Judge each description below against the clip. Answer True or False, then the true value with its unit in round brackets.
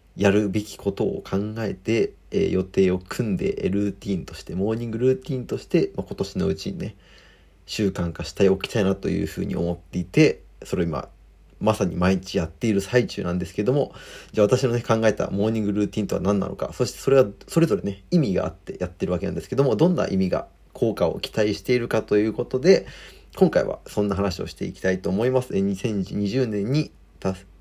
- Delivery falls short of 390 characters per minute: False (435 characters per minute)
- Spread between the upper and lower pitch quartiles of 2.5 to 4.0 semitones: True (2.9 semitones)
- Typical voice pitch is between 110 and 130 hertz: False (100 Hz)